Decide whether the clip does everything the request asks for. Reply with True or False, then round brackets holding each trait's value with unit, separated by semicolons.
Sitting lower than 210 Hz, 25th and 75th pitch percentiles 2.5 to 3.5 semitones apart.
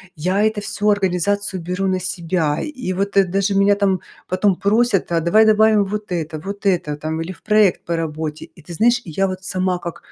True (190 Hz; 2.9 semitones)